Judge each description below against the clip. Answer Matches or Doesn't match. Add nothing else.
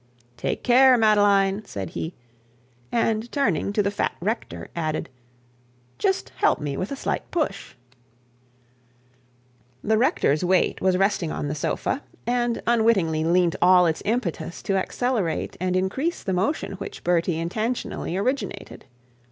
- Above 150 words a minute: Doesn't match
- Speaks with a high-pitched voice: Matches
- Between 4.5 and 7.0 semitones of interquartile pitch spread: Matches